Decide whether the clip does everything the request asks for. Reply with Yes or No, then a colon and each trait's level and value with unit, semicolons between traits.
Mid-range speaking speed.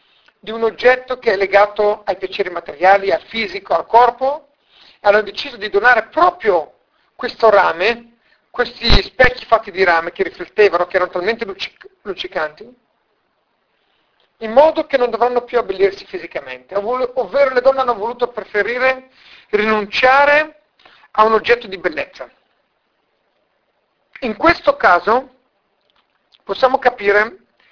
Yes: average, 125 wpm